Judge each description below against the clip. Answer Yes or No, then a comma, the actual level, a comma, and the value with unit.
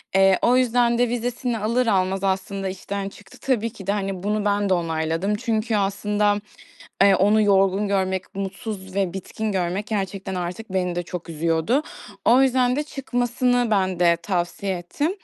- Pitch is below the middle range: No, high, 200 Hz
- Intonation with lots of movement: No, average, 3.3 semitones